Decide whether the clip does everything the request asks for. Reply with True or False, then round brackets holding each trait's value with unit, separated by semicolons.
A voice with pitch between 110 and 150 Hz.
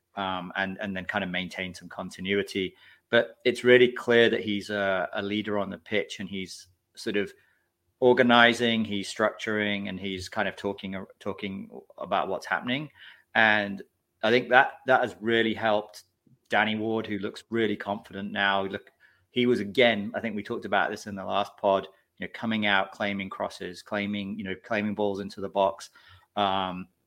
False (100 Hz)